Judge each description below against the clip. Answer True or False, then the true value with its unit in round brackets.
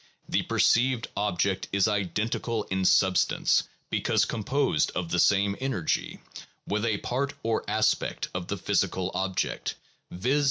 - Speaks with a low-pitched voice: True (100 Hz)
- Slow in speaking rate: True (130 wpm)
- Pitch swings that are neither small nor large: True (3.7 semitones)